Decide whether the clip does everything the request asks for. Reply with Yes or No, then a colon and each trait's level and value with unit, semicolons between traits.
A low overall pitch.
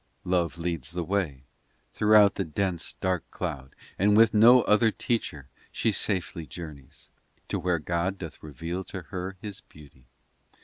Yes: very low, 90 Hz